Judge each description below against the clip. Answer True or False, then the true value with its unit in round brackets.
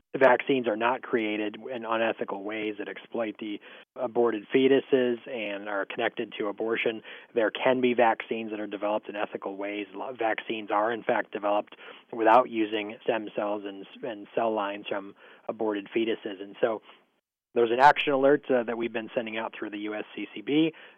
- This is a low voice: True (110 Hz)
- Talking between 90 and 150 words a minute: False (165 wpm)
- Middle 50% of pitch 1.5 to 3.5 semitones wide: True (2.8 semitones)